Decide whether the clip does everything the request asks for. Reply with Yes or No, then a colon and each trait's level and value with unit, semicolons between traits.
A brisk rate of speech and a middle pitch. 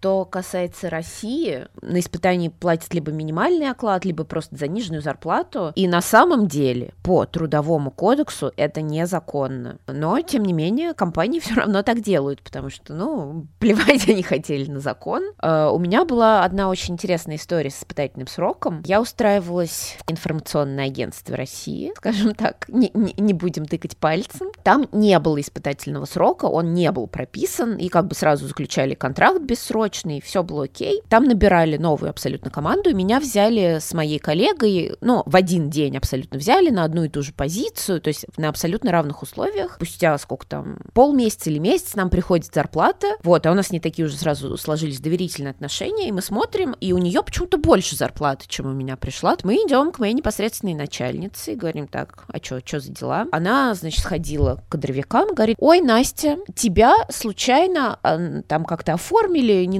Yes: fast, 175 wpm; medium, 175 Hz